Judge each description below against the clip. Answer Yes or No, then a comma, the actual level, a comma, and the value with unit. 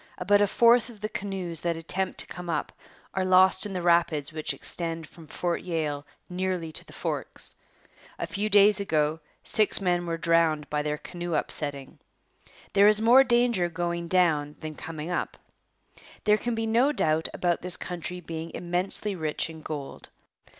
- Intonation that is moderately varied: Yes, average, 3.7 semitones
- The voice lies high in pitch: No, medium, 175 Hz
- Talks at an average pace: Yes, average, 170 wpm